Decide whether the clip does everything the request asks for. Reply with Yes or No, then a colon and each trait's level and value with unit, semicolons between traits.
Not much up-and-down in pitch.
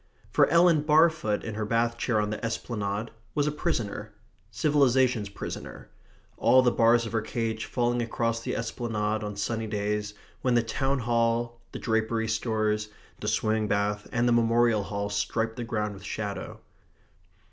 Yes: narrow, 2.2 semitones